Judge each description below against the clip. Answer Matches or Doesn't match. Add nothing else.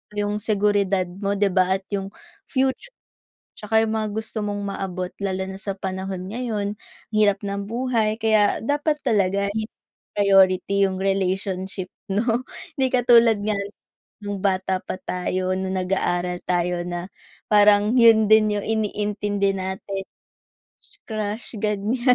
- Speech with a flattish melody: Matches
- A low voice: Doesn't match